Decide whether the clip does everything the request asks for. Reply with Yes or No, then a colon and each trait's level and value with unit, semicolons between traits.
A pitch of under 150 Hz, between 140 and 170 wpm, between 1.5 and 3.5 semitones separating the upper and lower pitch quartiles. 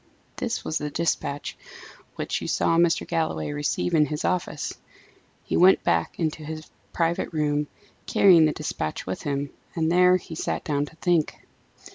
No: medium, 160 Hz; average, 160 wpm; narrow, 2.6 semitones